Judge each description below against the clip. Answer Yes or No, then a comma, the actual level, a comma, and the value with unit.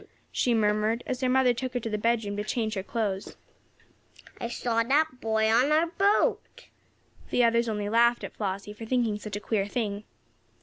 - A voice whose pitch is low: No, high, 230 Hz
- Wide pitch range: No, average, 2.8 semitones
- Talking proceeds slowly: No, average, 185 wpm